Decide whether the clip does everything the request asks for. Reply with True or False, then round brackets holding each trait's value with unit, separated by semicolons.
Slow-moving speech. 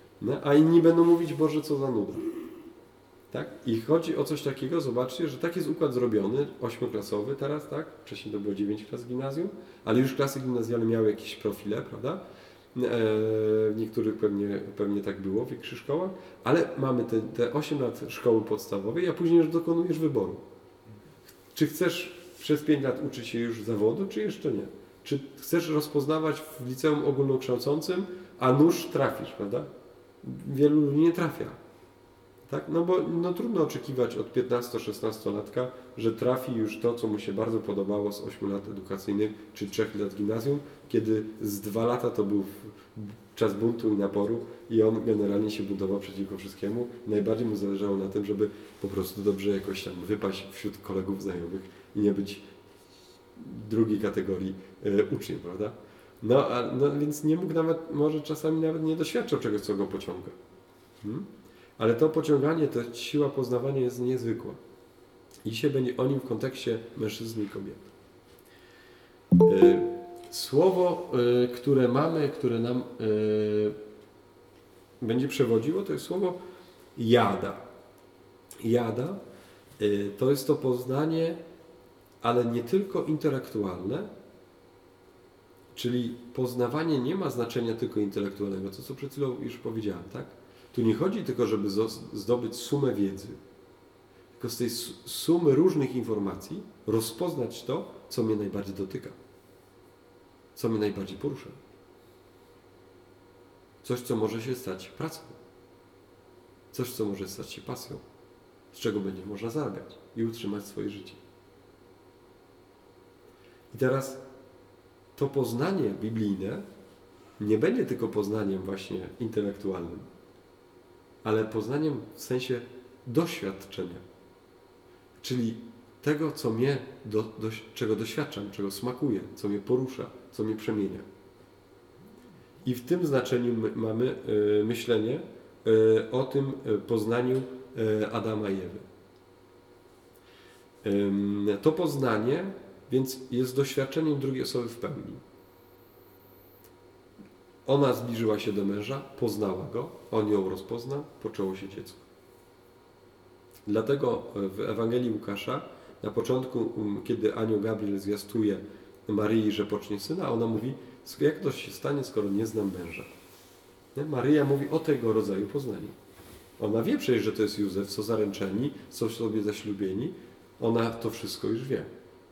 False (130 wpm)